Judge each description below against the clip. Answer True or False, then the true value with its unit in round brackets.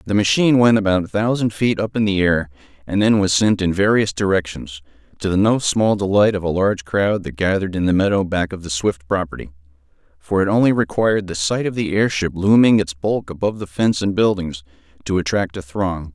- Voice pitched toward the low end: True (95 Hz)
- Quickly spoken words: True (215 wpm)